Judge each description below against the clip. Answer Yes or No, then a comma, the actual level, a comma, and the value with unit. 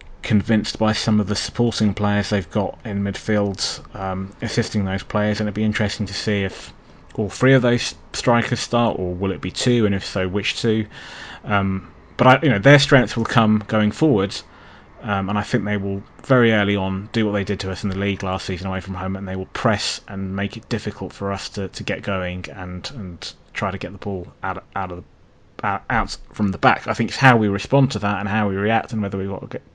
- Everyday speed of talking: No, fast, 240 wpm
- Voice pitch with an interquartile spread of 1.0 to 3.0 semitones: Yes, narrow, 2.5 semitones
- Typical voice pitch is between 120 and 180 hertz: No, low, 105 Hz